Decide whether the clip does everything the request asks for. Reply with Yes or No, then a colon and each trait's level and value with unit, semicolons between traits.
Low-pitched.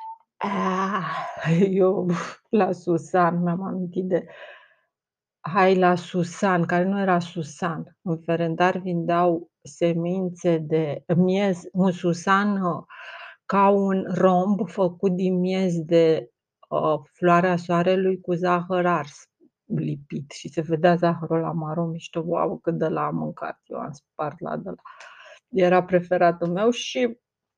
No: medium, 175 Hz